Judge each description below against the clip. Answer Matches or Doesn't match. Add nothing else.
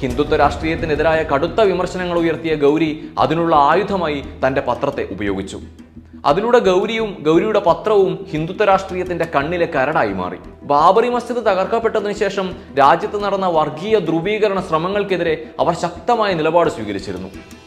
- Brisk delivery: Doesn't match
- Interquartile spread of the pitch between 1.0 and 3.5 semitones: Doesn't match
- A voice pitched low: Doesn't match